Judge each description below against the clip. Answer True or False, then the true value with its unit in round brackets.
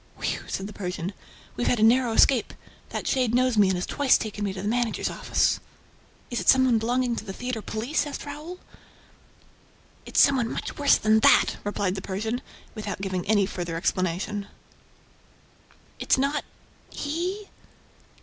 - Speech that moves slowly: False (170 wpm)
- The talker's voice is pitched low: False (220 Hz)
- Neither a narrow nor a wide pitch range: True (4.5 semitones)